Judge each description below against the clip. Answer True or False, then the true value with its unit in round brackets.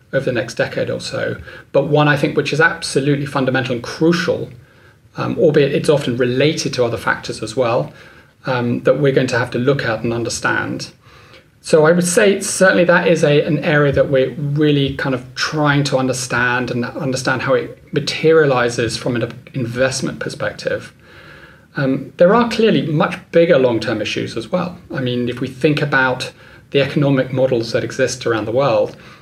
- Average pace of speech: True (185 wpm)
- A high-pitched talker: False (135 Hz)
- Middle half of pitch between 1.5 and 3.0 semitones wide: False (4.2 semitones)